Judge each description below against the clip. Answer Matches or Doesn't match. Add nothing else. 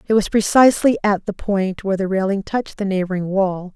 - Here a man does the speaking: Doesn't match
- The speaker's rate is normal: Doesn't match